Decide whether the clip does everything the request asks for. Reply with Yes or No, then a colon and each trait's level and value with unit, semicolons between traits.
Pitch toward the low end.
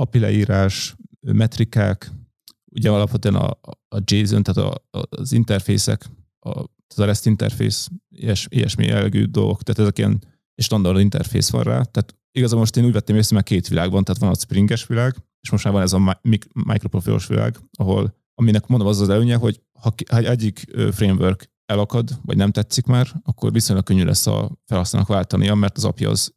Yes: low, 110 Hz